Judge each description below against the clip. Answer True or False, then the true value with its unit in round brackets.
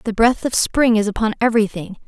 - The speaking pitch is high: True (220 Hz)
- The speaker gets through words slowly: False (205 wpm)